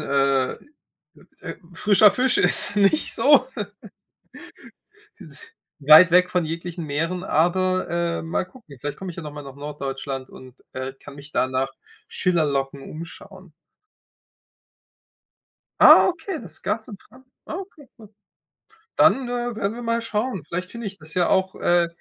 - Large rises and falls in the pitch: Yes, wide, 6.6 semitones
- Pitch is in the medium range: Yes, medium, 180 Hz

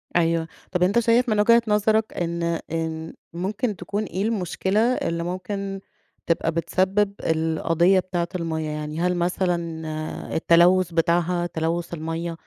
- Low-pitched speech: No, medium, 175 Hz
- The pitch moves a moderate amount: Yes, average, 3.0 semitones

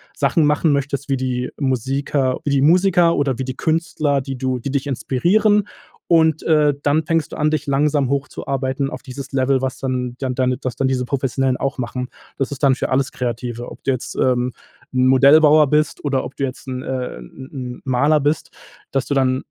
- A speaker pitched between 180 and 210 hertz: No, low, 135 Hz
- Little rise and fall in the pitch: Yes, narrow, 2.3 semitones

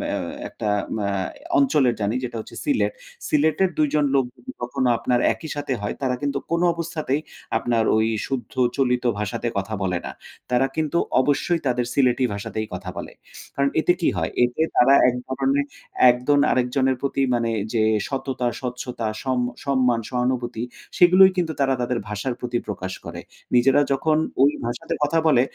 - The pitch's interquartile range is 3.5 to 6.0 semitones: No, average, 3.0 semitones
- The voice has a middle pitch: No, low, 130 Hz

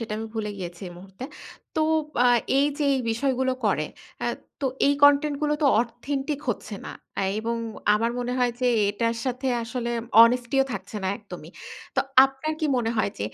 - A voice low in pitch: No, high, 245 Hz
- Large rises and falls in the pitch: No, average, 3.6 semitones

